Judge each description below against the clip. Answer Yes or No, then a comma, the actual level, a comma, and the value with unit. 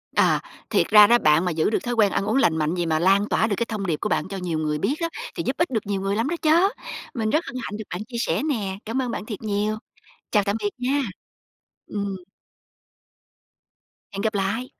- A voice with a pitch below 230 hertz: Yes, high, 210 Hz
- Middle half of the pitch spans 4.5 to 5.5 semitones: No, average, 3.8 semitones